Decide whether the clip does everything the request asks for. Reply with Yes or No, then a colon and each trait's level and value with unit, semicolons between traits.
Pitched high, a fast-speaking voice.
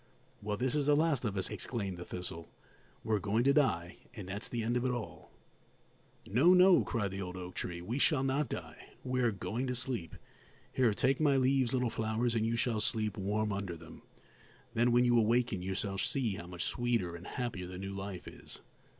No: low, 110 Hz; fast, 210 wpm